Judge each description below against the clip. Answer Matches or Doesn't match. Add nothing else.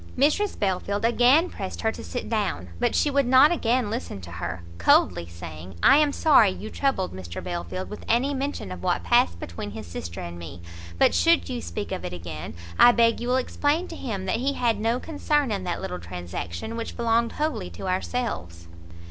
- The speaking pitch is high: Matches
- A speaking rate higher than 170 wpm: Matches